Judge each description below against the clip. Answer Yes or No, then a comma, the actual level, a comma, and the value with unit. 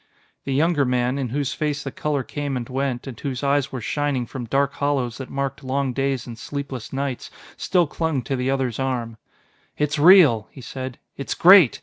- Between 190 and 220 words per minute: Yes, average, 195 wpm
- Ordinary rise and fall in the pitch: No, narrow, 2.2 semitones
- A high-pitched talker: No, low, 135 Hz